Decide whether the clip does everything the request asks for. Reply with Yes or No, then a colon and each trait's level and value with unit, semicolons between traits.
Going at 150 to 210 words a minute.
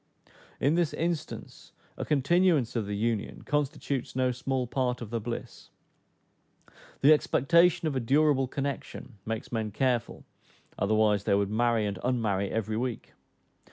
No: average, 140 wpm